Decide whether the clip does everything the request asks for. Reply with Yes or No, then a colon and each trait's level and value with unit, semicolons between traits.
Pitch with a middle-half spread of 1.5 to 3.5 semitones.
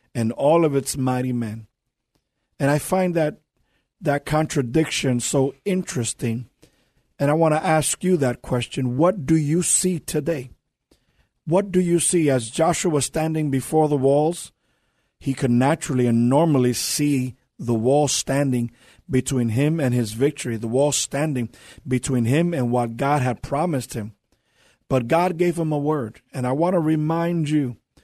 No: average, 4.2 semitones